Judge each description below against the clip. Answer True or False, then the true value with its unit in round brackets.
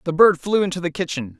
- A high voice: False (170 Hz)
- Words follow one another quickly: True (260 wpm)